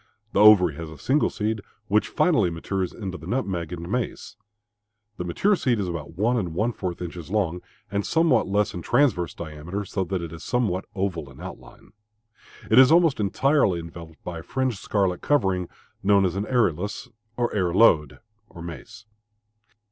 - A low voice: Yes, very low, 95 Hz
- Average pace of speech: Yes, average, 165 wpm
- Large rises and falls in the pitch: No, average, 4.5 semitones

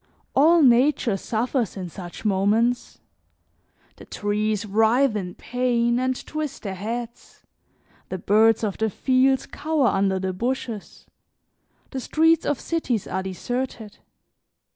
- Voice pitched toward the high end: Yes, high, 230 Hz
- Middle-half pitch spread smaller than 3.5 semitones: No, average, 4.1 semitones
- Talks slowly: Yes, slow, 120 wpm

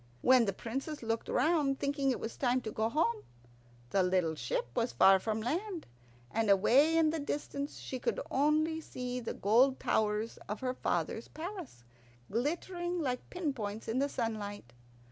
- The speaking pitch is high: Yes, very high, 255 Hz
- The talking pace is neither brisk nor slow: Yes, average, 165 wpm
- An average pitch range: No, wide, 5.7 semitones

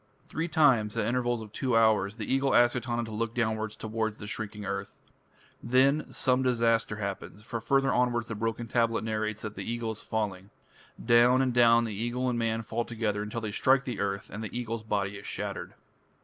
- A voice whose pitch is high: No, low, 115 Hz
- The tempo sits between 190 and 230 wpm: Yes, average, 195 wpm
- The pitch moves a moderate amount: No, narrow, 2.1 semitones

